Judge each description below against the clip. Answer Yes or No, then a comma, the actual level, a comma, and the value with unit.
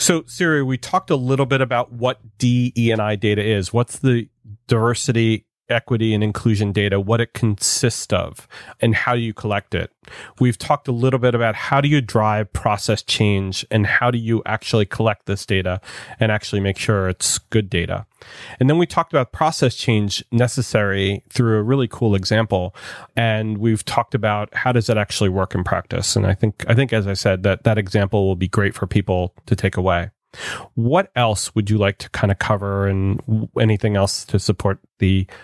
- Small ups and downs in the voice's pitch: No, average, 3.3 semitones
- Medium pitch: No, low, 110 Hz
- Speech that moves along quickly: No, average, 195 wpm